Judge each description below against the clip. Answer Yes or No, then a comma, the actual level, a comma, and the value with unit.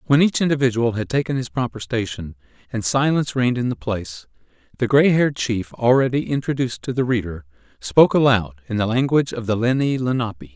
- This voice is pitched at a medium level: No, low, 120 Hz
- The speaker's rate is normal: Yes, average, 180 wpm